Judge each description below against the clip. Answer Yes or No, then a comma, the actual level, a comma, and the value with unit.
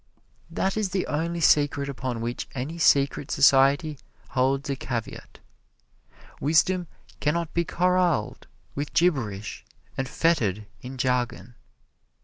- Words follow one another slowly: Yes, slow, 120 wpm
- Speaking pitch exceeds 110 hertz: Yes, medium, 140 Hz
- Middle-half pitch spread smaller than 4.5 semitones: No, average, 4.8 semitones